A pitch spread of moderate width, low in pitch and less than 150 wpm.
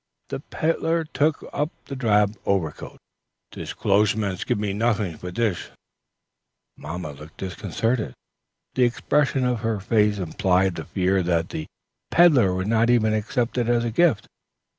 Yes: average, 4.5 semitones; low, 105 Hz; average, 140 wpm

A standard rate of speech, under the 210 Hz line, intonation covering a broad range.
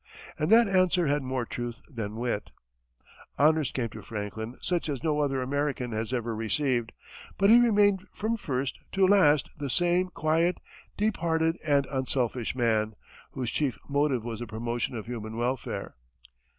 Yes: average, 160 wpm; low, 135 Hz; wide, 5.7 semitones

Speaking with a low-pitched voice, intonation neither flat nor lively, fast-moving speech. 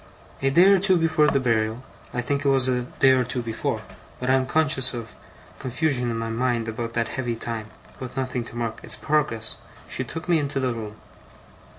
Yes: low, 125 Hz; average, 3.1 semitones; fast, 210 wpm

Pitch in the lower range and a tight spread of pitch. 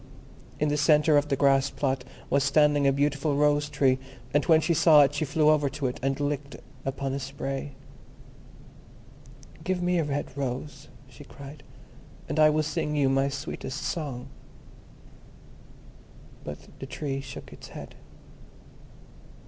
No: medium, 145 Hz; narrow, 1.6 semitones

